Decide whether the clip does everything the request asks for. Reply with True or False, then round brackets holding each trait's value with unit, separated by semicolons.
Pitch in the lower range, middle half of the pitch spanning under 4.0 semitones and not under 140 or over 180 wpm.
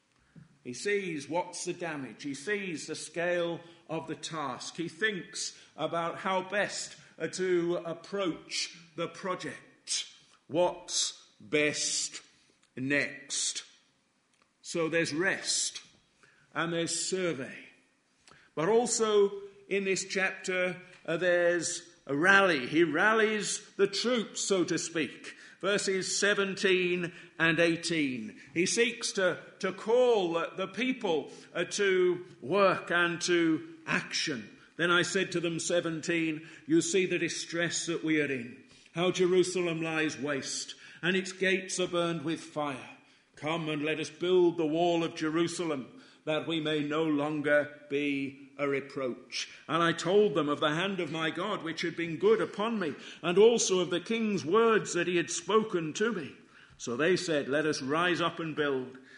False (170 Hz; 3.2 semitones; 145 wpm)